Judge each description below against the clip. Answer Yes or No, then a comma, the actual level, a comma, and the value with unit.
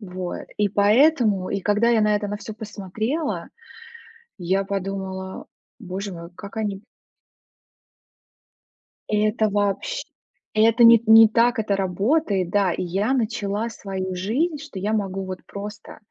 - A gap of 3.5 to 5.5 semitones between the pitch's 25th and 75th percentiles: No, narrow, 2.4 semitones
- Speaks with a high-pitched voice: Yes, high, 205 Hz